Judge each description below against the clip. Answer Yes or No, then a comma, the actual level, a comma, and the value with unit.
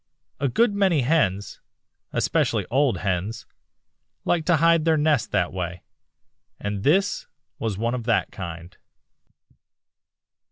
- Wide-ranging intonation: Yes, wide, 8.8 semitones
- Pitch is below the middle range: Yes, low, 120 Hz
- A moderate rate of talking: No, slow, 120 wpm